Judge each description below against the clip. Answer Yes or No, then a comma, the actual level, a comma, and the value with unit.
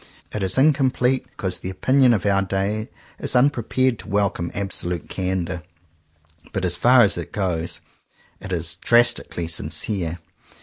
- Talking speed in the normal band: Yes, average, 145 wpm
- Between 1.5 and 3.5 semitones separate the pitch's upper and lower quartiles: No, average, 5.3 semitones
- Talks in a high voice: No, low, 100 Hz